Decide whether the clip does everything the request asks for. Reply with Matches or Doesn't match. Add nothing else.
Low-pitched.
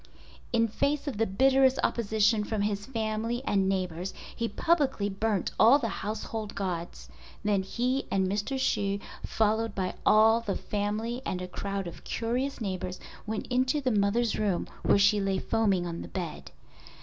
Doesn't match